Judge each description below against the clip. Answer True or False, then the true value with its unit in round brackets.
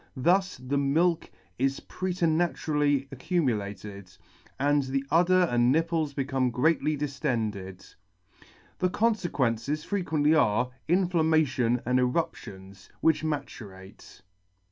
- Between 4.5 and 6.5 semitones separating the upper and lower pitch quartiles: True (4.9 semitones)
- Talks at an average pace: False (100 wpm)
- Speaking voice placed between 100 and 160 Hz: True (140 Hz)